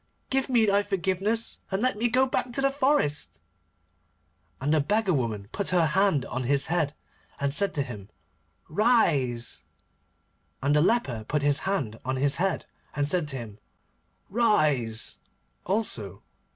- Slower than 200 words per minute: Yes, average, 150 wpm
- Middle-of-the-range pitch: Yes, medium, 155 Hz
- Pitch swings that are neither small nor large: No, wide, 7.9 semitones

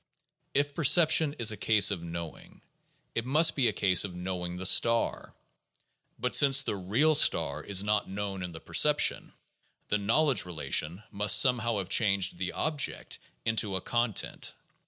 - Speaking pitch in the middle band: No, low, 105 Hz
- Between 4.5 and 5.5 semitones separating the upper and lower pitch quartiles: Yes, average, 5.1 semitones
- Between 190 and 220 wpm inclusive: No, average, 155 wpm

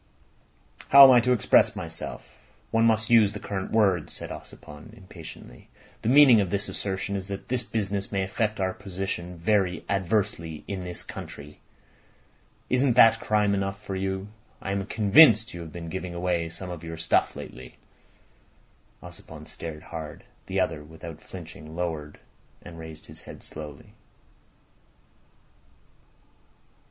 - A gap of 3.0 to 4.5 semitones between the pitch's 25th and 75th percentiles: Yes, average, 4.1 semitones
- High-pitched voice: No, very low, 95 Hz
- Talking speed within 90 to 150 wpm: Yes, average, 145 wpm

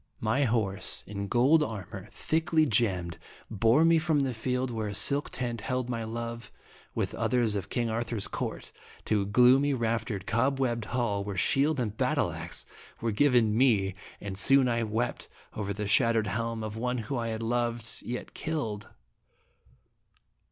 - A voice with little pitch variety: No, average, 3.0 semitones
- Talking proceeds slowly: No, average, 165 wpm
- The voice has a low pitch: Yes, low, 115 Hz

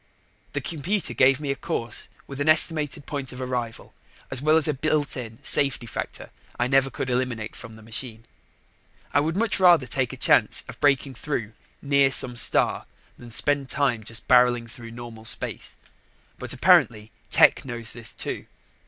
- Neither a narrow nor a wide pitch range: Yes, average, 3.5 semitones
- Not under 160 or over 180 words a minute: Yes, average, 170 wpm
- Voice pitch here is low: Yes, low, 130 Hz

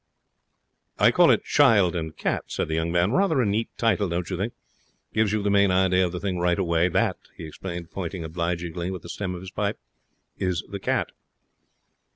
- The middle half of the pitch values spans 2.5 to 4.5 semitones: Yes, average, 2.8 semitones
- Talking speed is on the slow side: No, average, 200 wpm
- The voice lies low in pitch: Yes, very low, 90 Hz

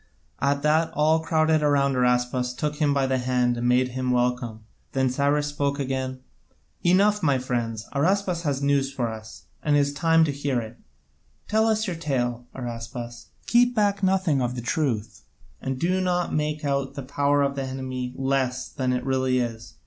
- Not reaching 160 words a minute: No, average, 185 wpm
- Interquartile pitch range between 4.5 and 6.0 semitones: No, average, 3.4 semitones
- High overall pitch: No, low, 135 Hz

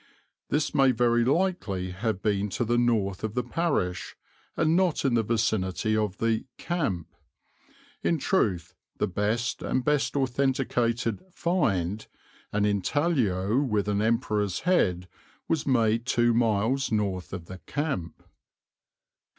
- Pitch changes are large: No, average, 5.0 semitones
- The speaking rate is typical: No, slow, 130 wpm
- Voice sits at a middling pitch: No, low, 115 Hz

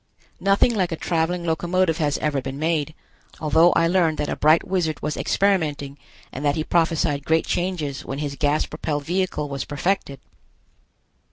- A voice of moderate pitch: Yes, medium, 160 Hz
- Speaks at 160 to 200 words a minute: Yes, average, 165 wpm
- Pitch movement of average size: Yes, average, 3.1 semitones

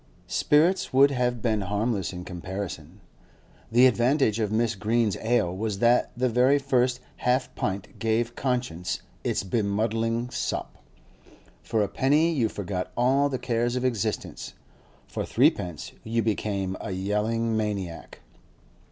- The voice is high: No, low, 115 Hz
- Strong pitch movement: No, average, 3.7 semitones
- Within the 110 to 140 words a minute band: Yes, slow, 135 wpm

